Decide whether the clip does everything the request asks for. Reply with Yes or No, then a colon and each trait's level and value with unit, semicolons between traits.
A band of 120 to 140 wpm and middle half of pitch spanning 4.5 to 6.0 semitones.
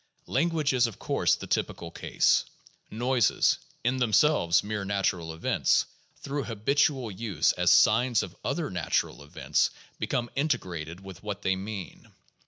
Yes: slow, 135 wpm; wide, 5.4 semitones